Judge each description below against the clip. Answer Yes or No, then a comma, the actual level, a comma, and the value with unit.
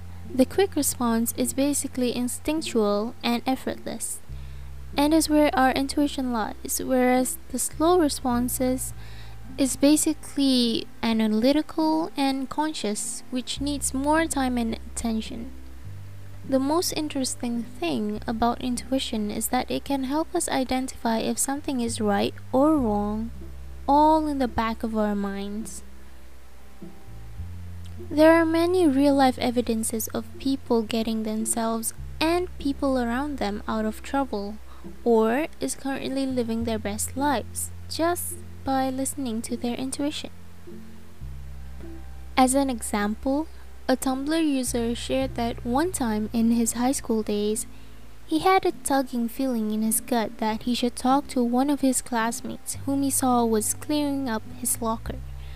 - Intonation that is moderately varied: Yes, average, 4.5 semitones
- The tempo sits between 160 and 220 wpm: No, slow, 135 wpm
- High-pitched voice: Yes, high, 240 Hz